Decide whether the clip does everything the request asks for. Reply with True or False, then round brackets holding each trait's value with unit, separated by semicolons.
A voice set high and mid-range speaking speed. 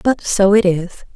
False (195 Hz; 210 wpm)